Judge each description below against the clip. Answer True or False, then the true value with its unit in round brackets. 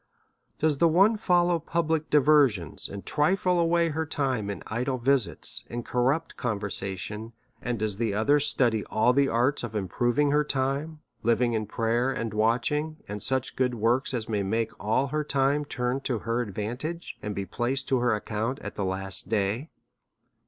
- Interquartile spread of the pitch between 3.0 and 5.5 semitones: True (5.1 semitones)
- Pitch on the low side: True (125 Hz)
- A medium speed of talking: True (175 wpm)